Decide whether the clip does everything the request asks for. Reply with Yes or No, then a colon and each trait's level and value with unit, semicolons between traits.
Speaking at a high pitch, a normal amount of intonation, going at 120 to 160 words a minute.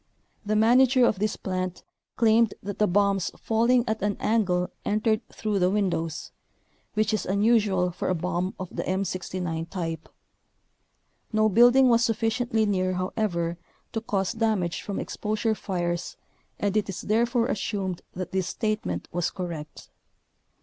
Yes: high, 205 Hz; average, 3.3 semitones; average, 145 wpm